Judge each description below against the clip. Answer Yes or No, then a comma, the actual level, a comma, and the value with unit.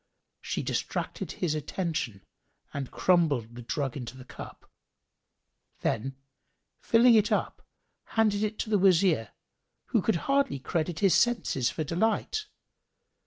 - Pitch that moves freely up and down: Yes, wide, 7.8 semitones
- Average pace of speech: No, slow, 125 wpm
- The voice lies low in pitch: No, medium, 170 Hz